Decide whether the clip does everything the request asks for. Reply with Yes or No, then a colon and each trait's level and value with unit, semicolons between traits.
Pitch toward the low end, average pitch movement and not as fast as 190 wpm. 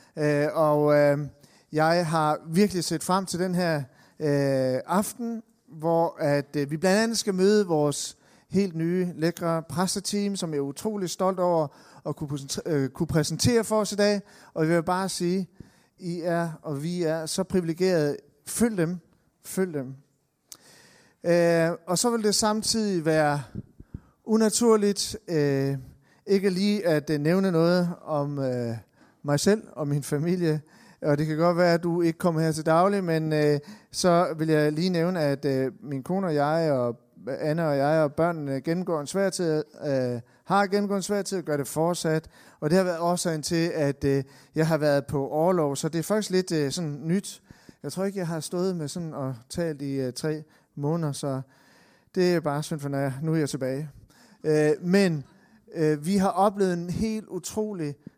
No: medium, 165 Hz; average, 4.0 semitones; average, 180 wpm